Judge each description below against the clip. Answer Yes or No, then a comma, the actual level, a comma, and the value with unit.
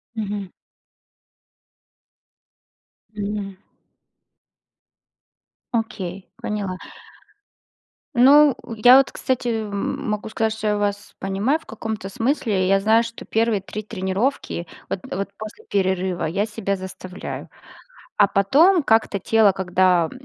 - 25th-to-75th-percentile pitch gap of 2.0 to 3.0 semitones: Yes, narrow, 2.6 semitones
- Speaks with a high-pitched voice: Yes, high, 205 Hz